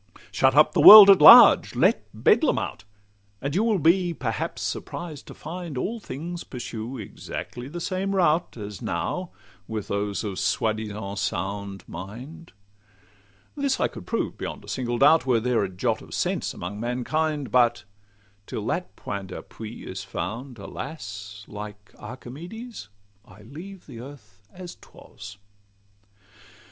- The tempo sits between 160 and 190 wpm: No, average, 145 wpm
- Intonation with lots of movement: Yes, wide, 7.9 semitones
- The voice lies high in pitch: No, low, 125 Hz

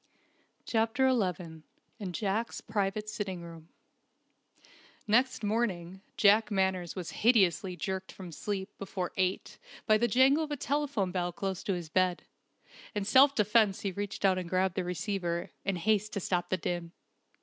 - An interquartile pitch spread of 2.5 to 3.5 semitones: Yes, average, 3.2 semitones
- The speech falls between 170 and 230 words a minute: No, average, 155 wpm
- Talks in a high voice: Yes, high, 195 Hz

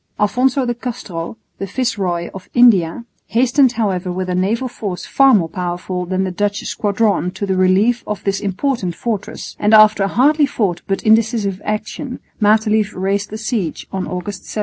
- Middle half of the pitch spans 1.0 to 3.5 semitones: No, average, 3.9 semitones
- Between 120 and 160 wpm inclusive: No, average, 170 wpm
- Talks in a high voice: Yes, high, 205 Hz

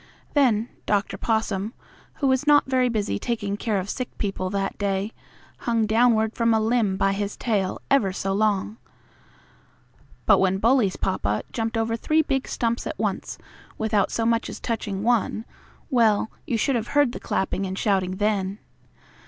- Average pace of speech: Yes, average, 165 wpm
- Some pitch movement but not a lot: Yes, average, 3.1 semitones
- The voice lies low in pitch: No, high, 220 Hz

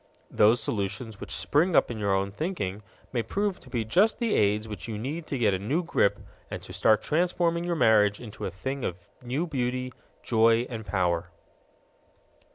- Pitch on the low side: Yes, low, 115 Hz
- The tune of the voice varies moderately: No, wide, 6.8 semitones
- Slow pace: No, average, 185 wpm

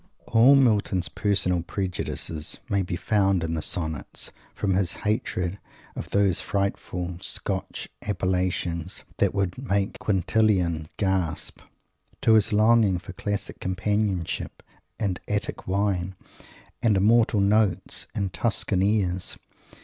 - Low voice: Yes, very low, 95 Hz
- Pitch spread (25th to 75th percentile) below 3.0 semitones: Yes, narrow, 2.5 semitones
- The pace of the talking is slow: Yes, slow, 115 wpm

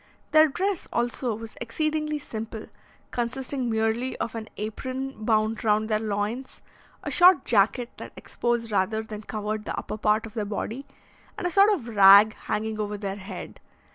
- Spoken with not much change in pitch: No, average, 3.4 semitones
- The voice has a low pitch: No, high, 225 Hz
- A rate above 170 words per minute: No, average, 165 wpm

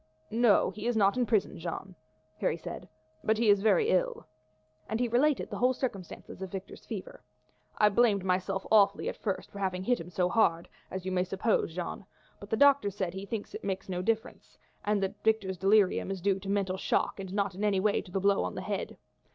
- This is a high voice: Yes, high, 200 Hz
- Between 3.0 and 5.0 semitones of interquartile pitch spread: No, narrow, 2.6 semitones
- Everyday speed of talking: No, fast, 220 wpm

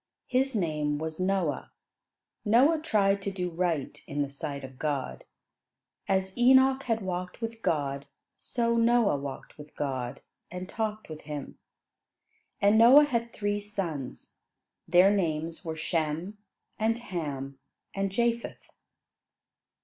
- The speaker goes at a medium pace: No, slow, 125 wpm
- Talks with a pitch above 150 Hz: Yes, medium, 185 Hz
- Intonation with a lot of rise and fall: Yes, wide, 6.9 semitones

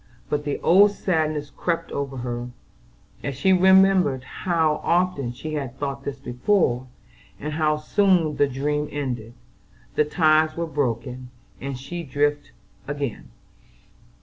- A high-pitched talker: No, medium, 145 Hz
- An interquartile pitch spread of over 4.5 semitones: No, average, 3.6 semitones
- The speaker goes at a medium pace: No, slow, 130 wpm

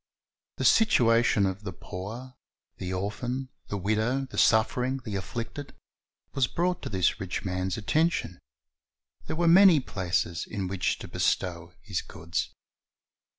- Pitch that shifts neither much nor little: No, wide, 5.8 semitones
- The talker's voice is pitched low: Yes, low, 105 Hz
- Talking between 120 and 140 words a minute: Yes, slow, 135 wpm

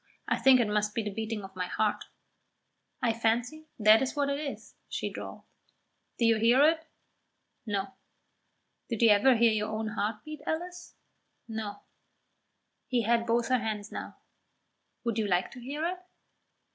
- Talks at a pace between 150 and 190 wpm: Yes, average, 165 wpm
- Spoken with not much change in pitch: No, average, 3.9 semitones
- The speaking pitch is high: Yes, high, 230 Hz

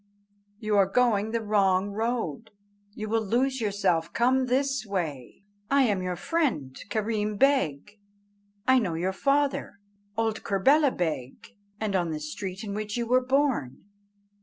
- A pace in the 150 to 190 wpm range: No, average, 140 wpm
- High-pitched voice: Yes, high, 215 Hz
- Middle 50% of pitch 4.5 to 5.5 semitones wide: Yes, average, 4.9 semitones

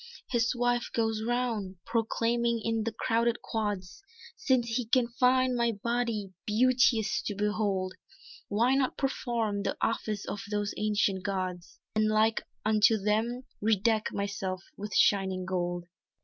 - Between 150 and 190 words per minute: No, slow, 135 wpm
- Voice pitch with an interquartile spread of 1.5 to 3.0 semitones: Yes, average, 2.7 semitones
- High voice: Yes, high, 220 Hz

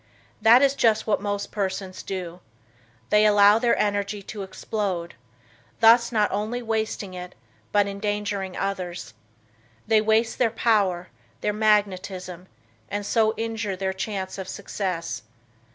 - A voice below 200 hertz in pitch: No, high, 205 Hz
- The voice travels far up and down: No, narrow, 2.5 semitones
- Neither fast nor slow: No, slow, 130 wpm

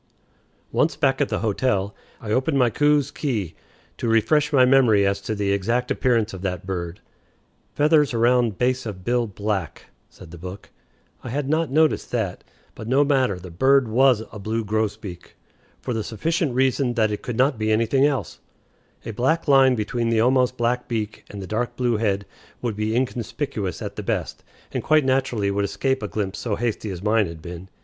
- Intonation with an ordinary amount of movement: Yes, average, 4.4 semitones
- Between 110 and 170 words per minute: No, average, 190 wpm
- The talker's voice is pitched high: No, low, 115 Hz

